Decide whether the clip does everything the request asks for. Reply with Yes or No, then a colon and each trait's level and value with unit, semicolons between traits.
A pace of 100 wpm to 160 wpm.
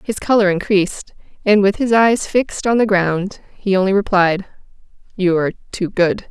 No: average, 170 wpm